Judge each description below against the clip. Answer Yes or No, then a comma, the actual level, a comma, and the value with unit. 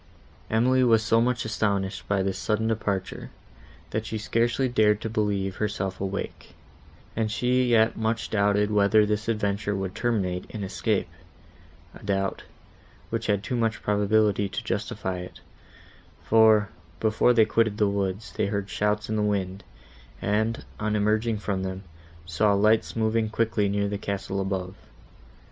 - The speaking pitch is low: Yes, low, 105 Hz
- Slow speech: No, average, 150 wpm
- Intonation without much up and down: Yes, narrow, 2.0 semitones